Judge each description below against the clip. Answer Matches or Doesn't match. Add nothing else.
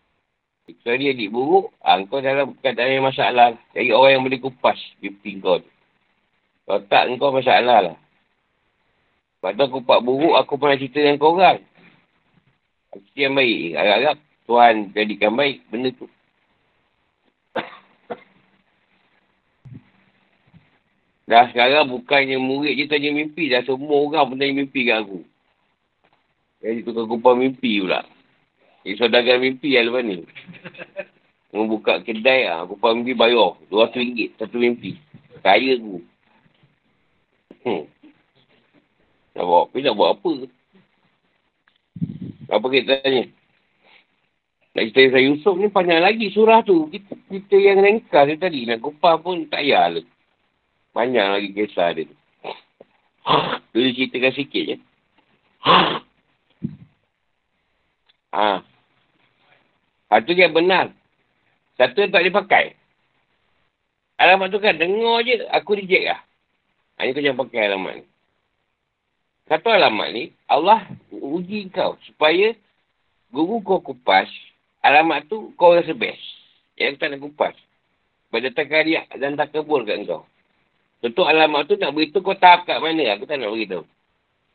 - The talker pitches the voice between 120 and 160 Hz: Matches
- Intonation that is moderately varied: Doesn't match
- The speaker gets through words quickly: Doesn't match